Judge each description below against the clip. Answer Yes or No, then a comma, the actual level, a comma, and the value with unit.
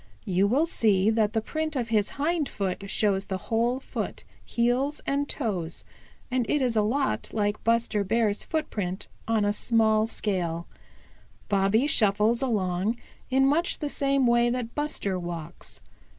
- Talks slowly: No, average, 150 wpm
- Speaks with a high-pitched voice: Yes, high, 225 Hz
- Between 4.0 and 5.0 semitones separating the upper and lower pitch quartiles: Yes, average, 4.5 semitones